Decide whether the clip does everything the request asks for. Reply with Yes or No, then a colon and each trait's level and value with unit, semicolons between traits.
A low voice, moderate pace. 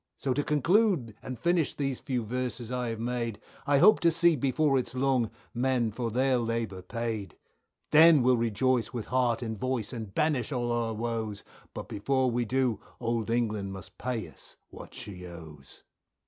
Yes: low, 120 Hz; average, 175 wpm